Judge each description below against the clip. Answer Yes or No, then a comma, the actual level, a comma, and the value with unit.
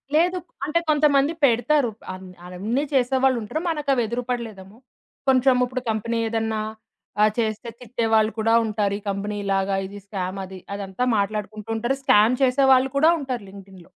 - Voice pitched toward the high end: Yes, high, 225 Hz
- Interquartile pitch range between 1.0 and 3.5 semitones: No, average, 4.4 semitones